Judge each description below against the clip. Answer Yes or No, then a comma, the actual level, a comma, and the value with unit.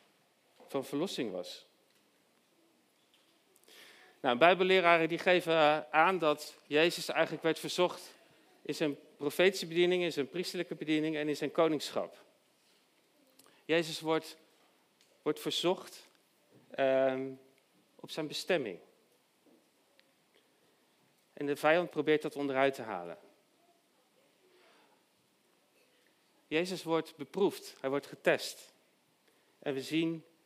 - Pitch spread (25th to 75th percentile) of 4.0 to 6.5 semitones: No, average, 2.8 semitones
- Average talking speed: No, slow, 100 wpm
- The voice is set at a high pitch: No, medium, 160 Hz